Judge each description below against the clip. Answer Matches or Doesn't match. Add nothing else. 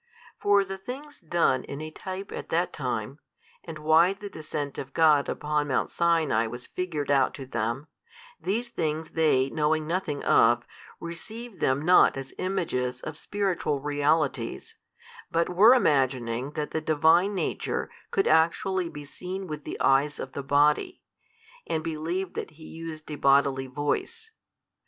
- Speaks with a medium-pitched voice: Matches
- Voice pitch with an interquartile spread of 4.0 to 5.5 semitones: Matches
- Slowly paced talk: Doesn't match